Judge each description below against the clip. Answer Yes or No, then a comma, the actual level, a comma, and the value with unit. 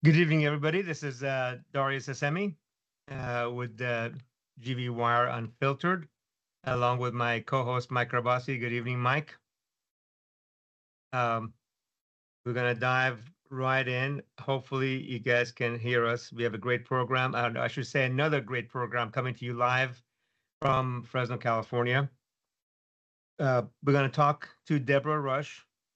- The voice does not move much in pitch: Yes, narrow, 2.0 semitones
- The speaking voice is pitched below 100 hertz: No, low, 125 Hz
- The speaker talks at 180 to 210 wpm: No, average, 150 wpm